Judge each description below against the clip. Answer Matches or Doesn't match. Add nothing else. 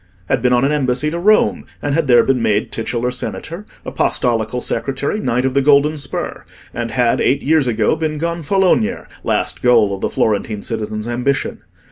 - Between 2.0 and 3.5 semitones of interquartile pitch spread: Doesn't match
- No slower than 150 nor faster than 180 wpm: Matches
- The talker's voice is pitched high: Doesn't match